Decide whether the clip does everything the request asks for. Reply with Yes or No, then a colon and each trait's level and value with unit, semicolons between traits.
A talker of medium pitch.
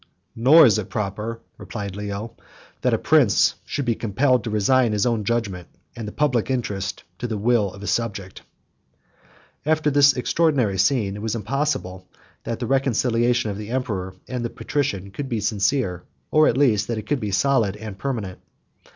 No: low, 115 Hz